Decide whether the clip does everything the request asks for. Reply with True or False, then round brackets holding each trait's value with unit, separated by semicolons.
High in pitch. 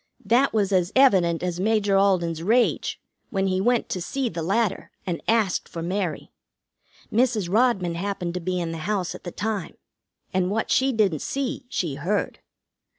True (195 Hz)